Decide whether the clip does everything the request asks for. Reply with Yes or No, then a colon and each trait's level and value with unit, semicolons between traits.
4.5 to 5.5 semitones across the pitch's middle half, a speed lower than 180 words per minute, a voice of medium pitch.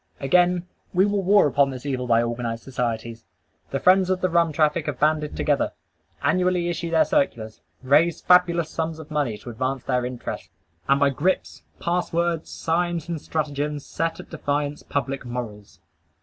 Yes: average, 4.9 semitones; average, 165 wpm; medium, 150 Hz